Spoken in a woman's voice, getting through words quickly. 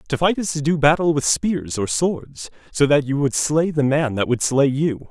No: male; fast, 245 wpm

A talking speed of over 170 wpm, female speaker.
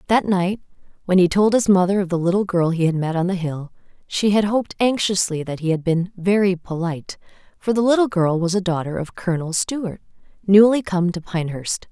Yes: fast, 205 wpm; female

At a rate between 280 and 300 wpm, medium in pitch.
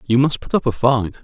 No: fast, 290 wpm; low, 125 Hz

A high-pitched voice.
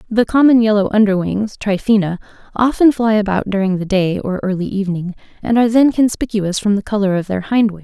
Yes: high, 205 Hz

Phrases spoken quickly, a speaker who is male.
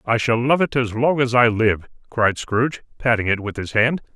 Yes: fast, 230 wpm; male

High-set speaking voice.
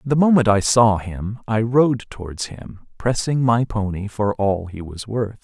No: low, 110 Hz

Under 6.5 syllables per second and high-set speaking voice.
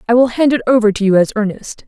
No: 6.8 syllables/s; high, 225 Hz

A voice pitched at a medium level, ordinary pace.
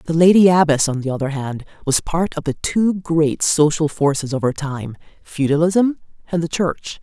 Yes: medium, 155 Hz; average, 190 wpm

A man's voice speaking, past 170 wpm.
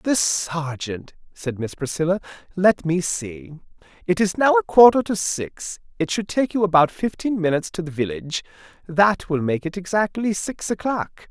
No: male; average, 165 wpm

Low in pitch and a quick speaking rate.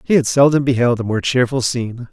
Yes: low, 125 Hz; fast, 225 wpm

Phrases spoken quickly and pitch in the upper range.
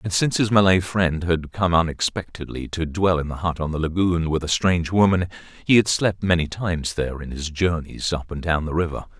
No: fast, 220 wpm; very low, 85 Hz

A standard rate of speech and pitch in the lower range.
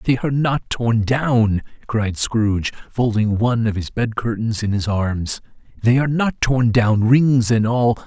Yes: average, 180 wpm; low, 115 Hz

